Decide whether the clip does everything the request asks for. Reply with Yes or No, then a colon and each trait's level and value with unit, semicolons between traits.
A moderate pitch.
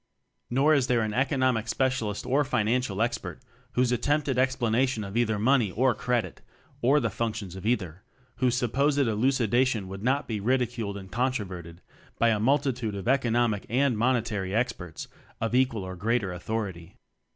No: low, 115 Hz